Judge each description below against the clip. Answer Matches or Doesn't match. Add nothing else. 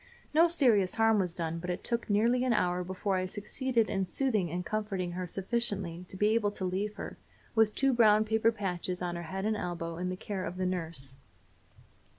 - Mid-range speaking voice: Doesn't match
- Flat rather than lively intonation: Doesn't match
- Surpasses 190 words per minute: Matches